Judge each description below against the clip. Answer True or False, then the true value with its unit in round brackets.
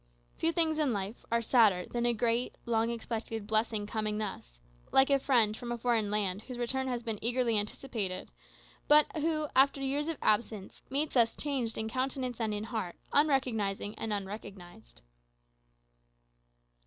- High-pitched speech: True (230 Hz)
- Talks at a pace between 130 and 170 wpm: True (155 wpm)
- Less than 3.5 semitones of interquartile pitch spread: False (3.8 semitones)